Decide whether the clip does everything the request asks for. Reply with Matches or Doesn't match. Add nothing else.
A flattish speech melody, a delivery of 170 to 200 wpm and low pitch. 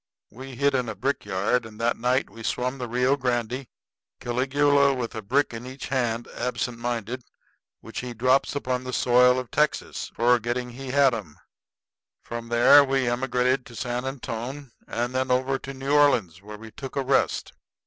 Matches